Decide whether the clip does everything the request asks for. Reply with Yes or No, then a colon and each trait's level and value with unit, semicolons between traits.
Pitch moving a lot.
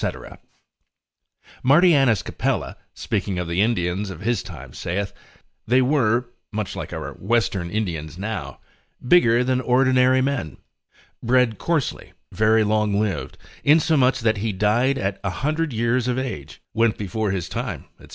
No: average, 4.5 semitones